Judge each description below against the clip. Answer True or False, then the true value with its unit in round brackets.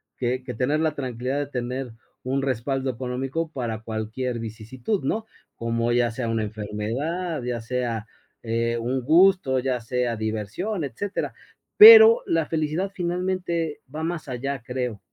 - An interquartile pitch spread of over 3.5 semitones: True (5.2 semitones)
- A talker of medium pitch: False (130 Hz)